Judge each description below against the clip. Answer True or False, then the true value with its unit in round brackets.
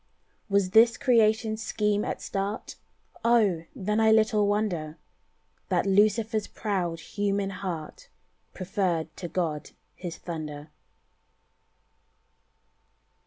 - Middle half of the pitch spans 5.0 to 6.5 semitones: False (3.8 semitones)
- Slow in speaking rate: True (95 wpm)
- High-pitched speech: True (200 Hz)